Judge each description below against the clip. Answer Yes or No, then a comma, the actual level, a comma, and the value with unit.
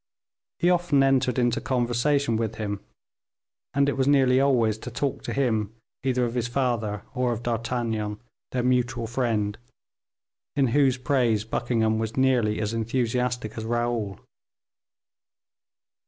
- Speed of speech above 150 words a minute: No, slow, 135 wpm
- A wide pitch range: No, average, 2.8 semitones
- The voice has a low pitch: Yes, low, 120 Hz